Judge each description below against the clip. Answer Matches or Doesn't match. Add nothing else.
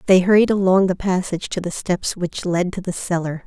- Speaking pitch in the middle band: Matches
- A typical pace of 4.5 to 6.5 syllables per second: Matches